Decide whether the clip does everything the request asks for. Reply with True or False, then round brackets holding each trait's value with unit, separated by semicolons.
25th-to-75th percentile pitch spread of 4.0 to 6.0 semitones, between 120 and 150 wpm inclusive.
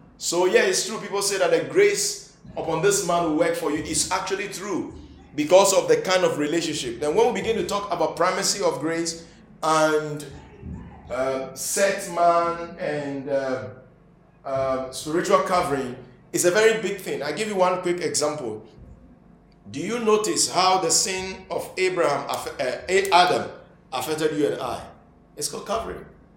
False (4.6 semitones; 165 wpm)